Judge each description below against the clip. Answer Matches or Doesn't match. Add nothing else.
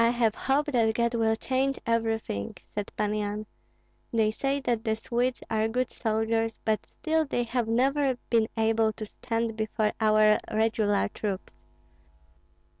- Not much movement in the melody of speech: Matches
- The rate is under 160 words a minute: Matches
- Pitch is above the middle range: Matches